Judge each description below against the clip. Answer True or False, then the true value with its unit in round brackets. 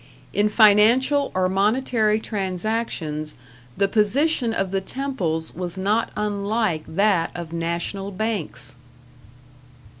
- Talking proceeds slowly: True (100 wpm)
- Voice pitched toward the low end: False (200 Hz)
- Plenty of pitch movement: False (3.8 semitones)